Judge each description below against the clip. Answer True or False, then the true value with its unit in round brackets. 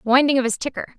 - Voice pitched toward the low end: False (260 Hz)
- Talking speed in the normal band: False (245 wpm)